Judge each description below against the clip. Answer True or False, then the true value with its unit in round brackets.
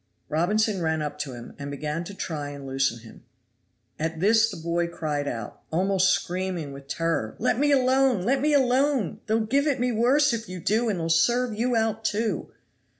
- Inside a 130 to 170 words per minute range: False (195 wpm)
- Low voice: False (190 Hz)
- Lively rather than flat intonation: True (7.1 semitones)